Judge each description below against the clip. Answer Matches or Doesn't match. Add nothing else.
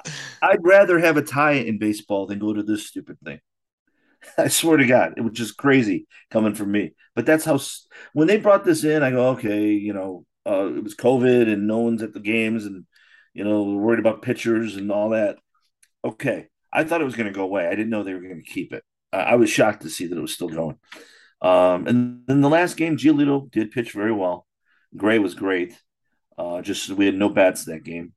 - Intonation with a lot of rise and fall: Matches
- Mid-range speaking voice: Doesn't match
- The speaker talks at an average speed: Doesn't match